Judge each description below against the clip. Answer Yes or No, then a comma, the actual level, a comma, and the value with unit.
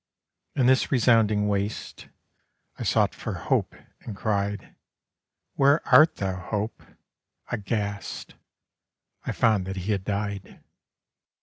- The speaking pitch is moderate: No, low, 105 Hz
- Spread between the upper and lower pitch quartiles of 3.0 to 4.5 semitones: No, narrow, 2.6 semitones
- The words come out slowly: Yes, slow, 105 wpm